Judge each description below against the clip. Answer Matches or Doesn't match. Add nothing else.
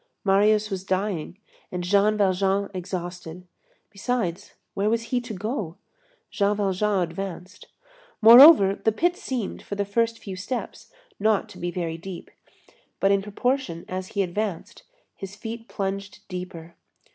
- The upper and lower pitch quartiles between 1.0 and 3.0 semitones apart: Matches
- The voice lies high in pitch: Matches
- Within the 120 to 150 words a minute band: Matches